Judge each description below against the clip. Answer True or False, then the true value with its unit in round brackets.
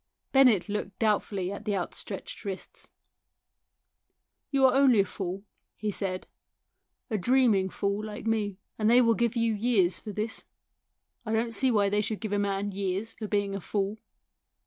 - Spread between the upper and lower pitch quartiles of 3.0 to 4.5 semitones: False (2.4 semitones)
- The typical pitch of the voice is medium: False (210 Hz)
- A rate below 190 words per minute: True (175 wpm)